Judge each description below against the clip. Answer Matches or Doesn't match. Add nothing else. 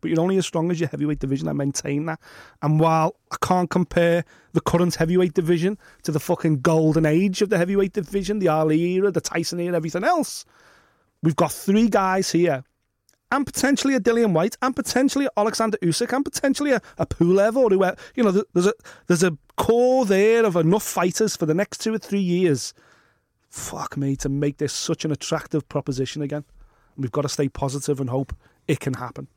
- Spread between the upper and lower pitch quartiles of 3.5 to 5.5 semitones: Matches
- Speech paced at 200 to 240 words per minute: Matches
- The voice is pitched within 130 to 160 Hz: Doesn't match